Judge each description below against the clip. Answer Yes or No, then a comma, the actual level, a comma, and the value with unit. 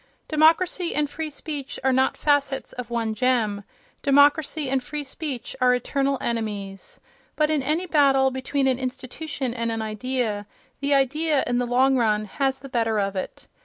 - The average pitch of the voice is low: No, very high, 265 Hz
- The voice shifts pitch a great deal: No, average, 3.5 semitones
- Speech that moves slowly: No, average, 165 wpm